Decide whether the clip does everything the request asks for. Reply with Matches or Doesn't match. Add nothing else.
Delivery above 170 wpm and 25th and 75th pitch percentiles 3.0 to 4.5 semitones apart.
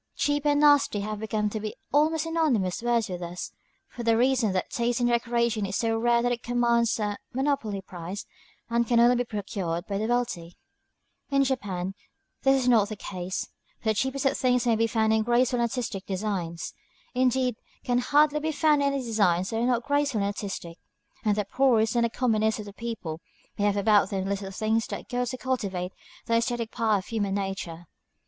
Matches